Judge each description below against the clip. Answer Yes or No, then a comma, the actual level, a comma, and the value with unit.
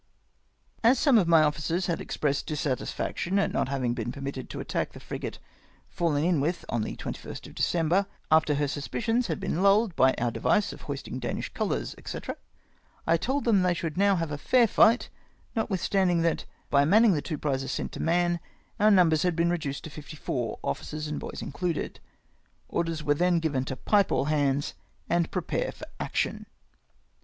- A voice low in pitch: No, medium, 165 Hz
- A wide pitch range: No, average, 4.5 semitones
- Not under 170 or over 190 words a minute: Yes, average, 185 wpm